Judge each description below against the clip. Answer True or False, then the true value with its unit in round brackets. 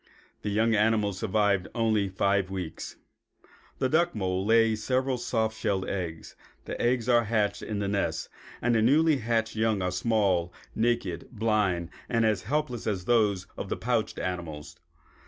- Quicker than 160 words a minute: False (155 wpm)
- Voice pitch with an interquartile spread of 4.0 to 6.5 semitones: False (3.3 semitones)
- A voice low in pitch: True (110 Hz)